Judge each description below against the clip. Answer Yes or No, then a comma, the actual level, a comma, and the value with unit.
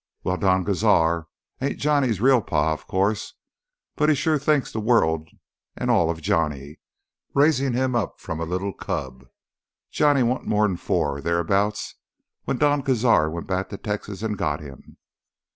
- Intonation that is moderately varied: No, wide, 7.6 semitones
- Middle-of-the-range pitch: No, low, 100 Hz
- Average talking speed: Yes, average, 160 wpm